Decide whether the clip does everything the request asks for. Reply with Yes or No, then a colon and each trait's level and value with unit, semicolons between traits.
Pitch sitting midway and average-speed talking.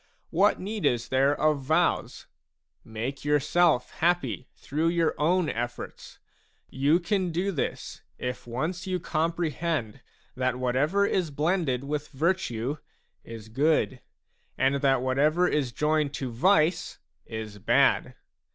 No: medium, 150 Hz; slow, 125 wpm